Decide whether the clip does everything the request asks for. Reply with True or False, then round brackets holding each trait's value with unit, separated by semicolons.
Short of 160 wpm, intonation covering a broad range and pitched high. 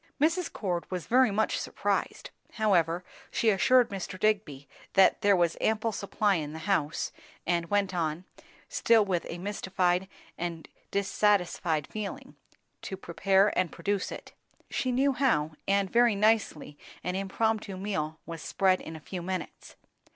False (145 wpm; 3.7 semitones; 195 Hz)